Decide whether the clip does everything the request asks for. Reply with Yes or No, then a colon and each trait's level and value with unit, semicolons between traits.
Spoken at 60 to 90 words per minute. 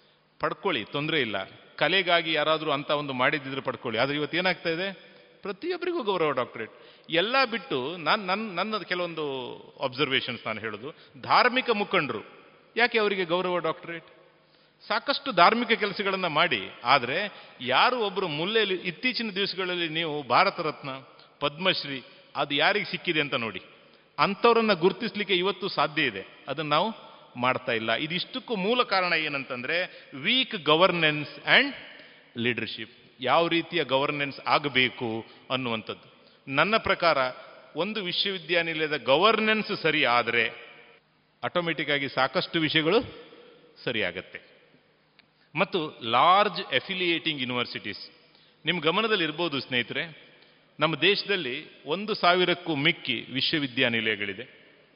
No: fast, 105 wpm